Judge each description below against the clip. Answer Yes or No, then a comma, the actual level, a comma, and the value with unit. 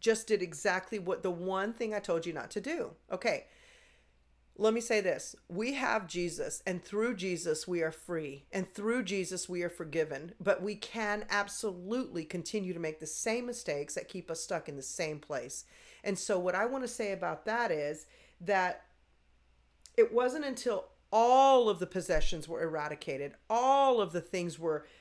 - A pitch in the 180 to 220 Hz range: Yes, medium, 185 Hz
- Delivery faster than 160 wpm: Yes, average, 180 wpm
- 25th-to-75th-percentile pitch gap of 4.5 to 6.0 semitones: Yes, average, 5.0 semitones